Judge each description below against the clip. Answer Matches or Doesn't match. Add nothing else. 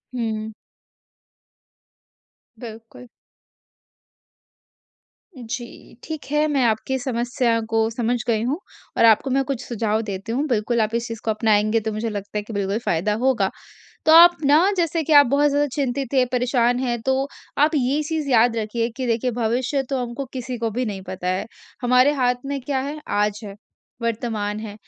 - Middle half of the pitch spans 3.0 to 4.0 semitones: Matches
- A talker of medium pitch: Doesn't match